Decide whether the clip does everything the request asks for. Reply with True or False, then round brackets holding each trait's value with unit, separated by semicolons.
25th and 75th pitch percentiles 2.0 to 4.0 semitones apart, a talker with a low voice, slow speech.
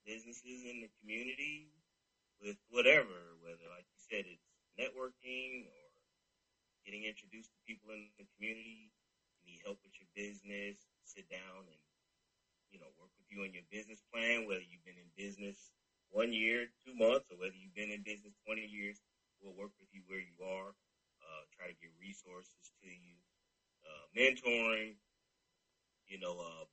False (3.1 semitones; 105 Hz; 165 wpm)